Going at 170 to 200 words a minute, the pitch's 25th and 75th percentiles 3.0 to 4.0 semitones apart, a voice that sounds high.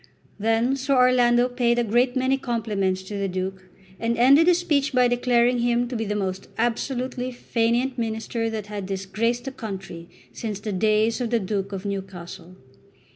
Yes: average, 175 wpm; average, 3.7 semitones; high, 230 Hz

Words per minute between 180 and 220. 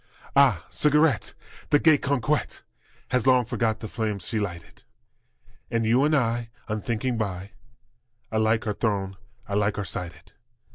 No: slow, 135 wpm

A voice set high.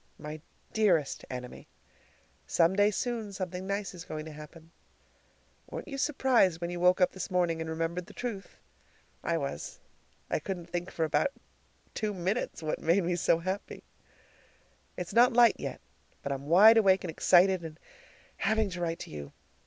No: medium, 180 Hz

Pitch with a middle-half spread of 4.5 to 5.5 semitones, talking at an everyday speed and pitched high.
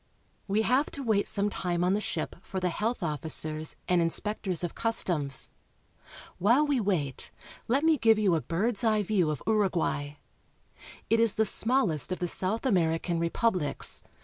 Yes: average, 5.0 semitones; average, 165 wpm; high, 195 Hz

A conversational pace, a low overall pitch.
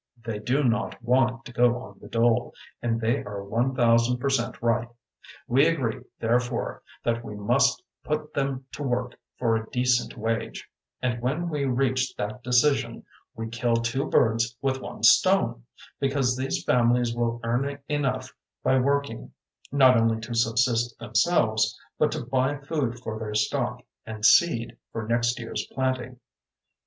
Yes: average, 155 wpm; low, 120 Hz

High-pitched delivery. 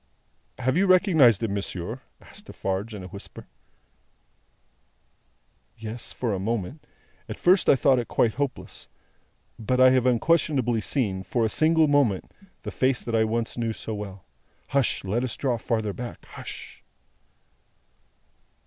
No: low, 120 Hz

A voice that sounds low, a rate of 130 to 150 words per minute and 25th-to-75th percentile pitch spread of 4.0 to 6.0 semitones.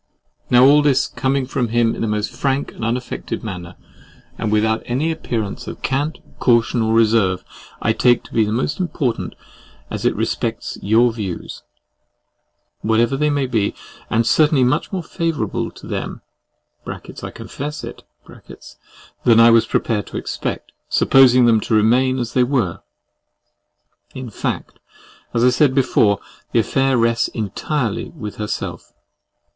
No: low, 120 Hz; average, 145 wpm; average, 3.3 semitones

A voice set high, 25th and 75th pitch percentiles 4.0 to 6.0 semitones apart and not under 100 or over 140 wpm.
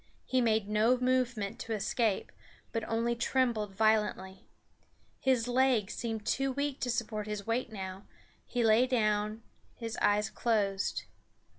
No: high, 225 Hz; average, 2.7 semitones; slow, 135 wpm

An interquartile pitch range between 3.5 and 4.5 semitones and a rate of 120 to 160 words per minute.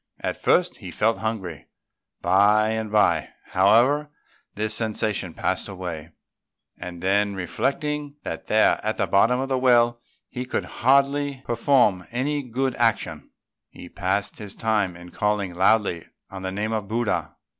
Yes: average, 4.2 semitones; average, 145 wpm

